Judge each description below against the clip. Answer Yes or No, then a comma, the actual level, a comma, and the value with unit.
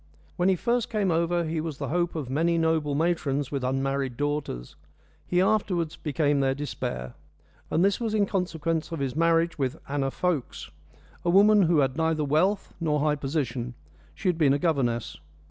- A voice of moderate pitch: Yes, medium, 155 Hz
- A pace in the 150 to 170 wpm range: No, average, 180 wpm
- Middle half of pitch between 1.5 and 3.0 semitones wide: No, average, 3.9 semitones